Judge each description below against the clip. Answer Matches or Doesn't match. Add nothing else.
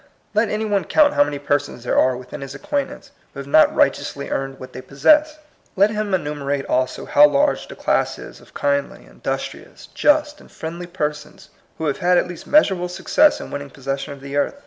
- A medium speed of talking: Doesn't match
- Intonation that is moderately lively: Doesn't match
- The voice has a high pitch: Doesn't match